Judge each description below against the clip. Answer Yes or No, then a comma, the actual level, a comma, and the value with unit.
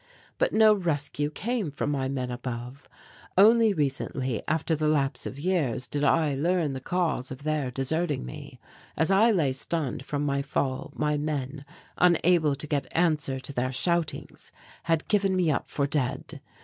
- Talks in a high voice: No, medium, 150 Hz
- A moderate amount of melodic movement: Yes, average, 4.0 semitones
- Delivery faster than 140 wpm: Yes, average, 165 wpm